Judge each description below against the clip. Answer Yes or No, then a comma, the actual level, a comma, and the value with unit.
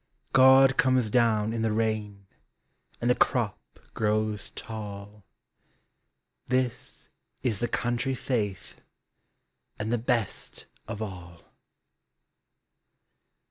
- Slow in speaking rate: Yes, slow, 100 wpm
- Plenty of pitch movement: No, average, 2.9 semitones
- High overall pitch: No, low, 110 Hz